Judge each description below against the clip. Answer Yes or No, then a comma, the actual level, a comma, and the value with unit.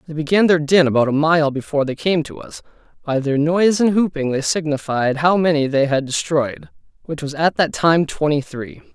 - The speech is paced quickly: Yes, fast, 210 wpm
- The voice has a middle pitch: Yes, medium, 155 Hz